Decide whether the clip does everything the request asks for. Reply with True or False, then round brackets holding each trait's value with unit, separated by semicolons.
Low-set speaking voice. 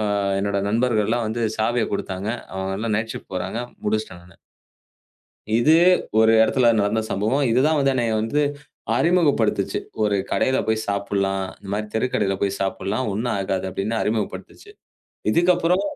True (110 Hz)